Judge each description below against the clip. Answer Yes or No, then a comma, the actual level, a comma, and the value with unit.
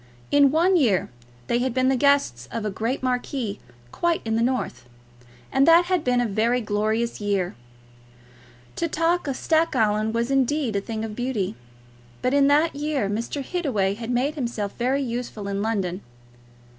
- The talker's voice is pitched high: Yes, high, 245 Hz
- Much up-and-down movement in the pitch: No, average, 4.8 semitones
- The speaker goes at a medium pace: Yes, average, 170 wpm